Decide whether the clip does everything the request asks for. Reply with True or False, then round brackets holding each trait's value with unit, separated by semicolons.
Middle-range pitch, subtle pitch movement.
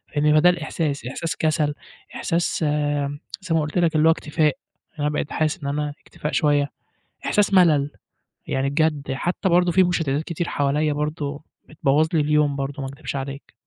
True (150 Hz; 2.3 semitones)